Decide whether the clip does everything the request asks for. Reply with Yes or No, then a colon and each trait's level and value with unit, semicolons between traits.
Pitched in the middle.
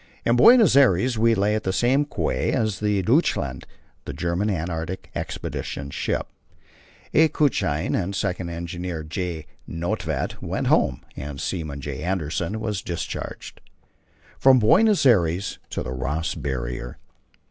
No: very low, 90 Hz